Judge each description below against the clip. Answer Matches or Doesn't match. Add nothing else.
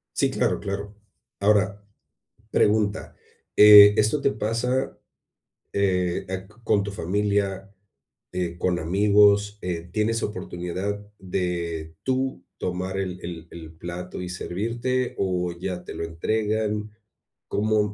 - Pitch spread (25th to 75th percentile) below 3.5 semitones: Matches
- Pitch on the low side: Matches